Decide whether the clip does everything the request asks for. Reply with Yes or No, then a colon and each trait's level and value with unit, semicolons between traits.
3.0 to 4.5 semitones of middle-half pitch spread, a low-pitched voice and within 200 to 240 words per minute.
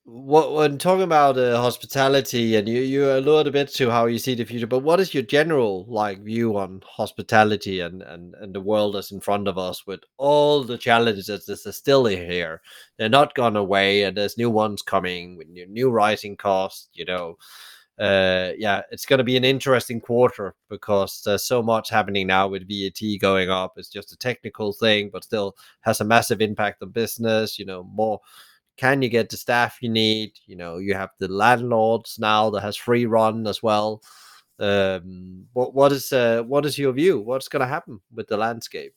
Yes: average, 4.0 semitones; low, 110 Hz; fast, 205 wpm